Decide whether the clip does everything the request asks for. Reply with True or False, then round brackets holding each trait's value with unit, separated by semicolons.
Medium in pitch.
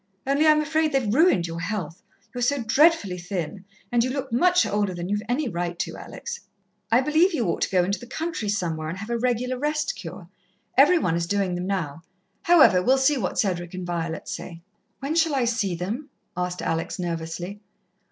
False (210 Hz)